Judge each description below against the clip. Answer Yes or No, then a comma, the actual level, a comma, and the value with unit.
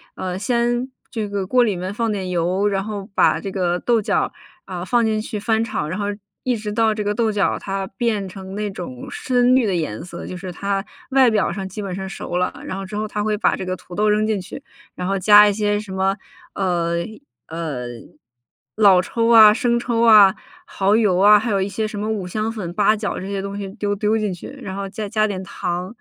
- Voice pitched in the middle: No, high, 205 Hz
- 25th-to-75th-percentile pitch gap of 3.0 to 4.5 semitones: No, narrow, 2.5 semitones